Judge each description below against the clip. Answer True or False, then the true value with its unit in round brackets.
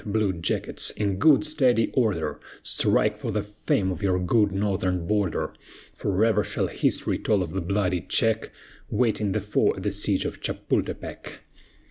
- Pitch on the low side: True (105 Hz)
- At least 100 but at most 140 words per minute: False (155 wpm)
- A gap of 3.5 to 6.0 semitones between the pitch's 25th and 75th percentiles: False (2.7 semitones)